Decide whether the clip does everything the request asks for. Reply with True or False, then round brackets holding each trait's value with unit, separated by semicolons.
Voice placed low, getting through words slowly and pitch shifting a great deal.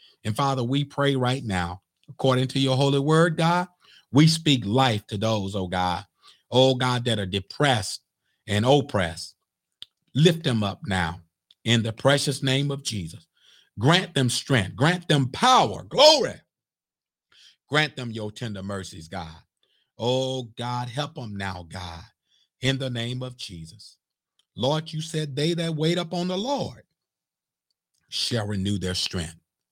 False (125 Hz; 145 wpm; 6.4 semitones)